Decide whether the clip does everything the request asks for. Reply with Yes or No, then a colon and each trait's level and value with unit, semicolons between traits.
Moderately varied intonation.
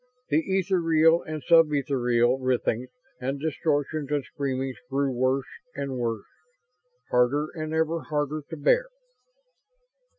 Yes: average, 3.3 semitones